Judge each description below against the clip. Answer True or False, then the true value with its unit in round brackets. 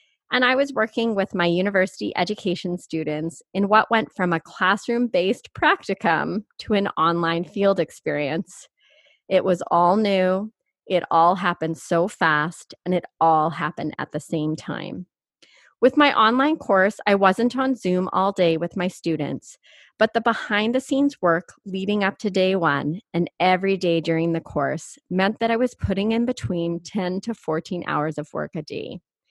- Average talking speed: True (170 wpm)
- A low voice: False (185 Hz)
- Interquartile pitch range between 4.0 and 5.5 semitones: True (4.6 semitones)